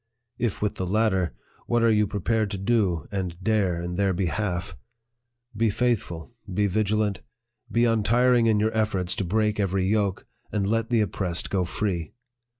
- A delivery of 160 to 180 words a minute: Yes, average, 165 wpm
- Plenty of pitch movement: No, average, 3.0 semitones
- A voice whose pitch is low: Yes, low, 105 Hz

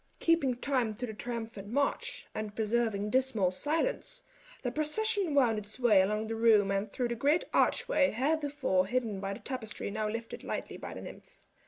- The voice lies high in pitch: Yes, high, 235 Hz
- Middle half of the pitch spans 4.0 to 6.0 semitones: Yes, average, 4.7 semitones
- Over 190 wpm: No, average, 175 wpm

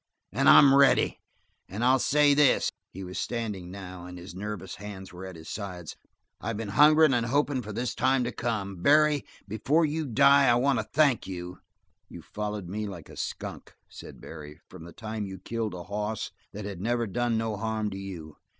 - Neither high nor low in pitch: No, low, 105 Hz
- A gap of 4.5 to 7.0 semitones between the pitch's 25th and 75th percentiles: Yes, average, 4.8 semitones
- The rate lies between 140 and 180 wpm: No, average, 195 wpm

